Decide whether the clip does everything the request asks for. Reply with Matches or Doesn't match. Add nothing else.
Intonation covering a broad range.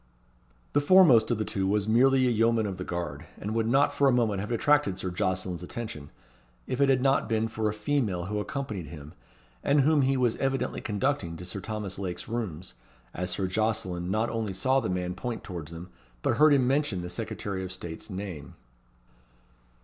Matches